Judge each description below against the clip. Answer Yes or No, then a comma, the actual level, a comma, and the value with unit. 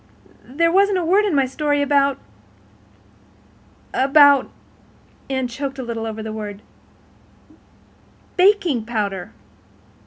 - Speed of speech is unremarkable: No, slow, 95 wpm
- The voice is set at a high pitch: Yes, very high, 250 Hz